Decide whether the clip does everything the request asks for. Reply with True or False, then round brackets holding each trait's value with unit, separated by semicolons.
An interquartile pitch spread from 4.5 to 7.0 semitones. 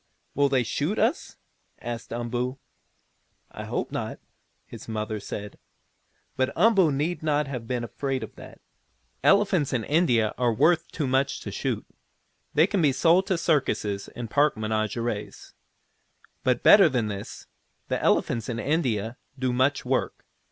True (5.0 semitones)